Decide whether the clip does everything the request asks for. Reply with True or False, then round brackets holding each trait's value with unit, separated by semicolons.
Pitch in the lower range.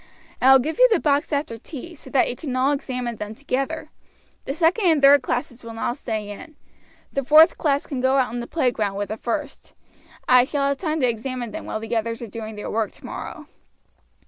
False (255 Hz)